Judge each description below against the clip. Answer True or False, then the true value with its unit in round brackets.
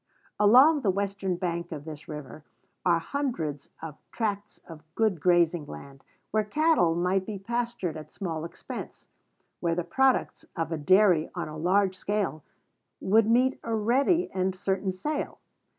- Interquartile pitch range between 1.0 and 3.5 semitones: False (4.9 semitones)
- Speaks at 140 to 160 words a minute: True (150 wpm)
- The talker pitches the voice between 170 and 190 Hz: True (185 Hz)